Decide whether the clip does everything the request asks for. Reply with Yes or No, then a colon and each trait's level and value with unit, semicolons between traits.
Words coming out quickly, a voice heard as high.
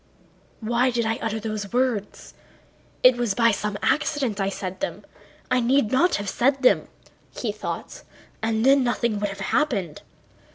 No: average, 160 wpm; high, 230 Hz